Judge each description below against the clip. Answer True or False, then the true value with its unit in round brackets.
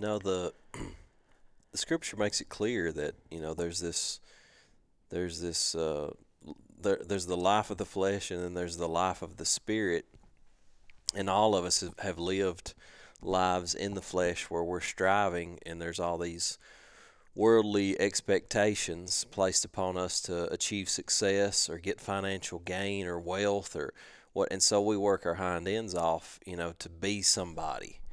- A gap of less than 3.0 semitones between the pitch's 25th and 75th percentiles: True (2.5 semitones)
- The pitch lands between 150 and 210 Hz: False (95 Hz)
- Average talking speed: True (165 wpm)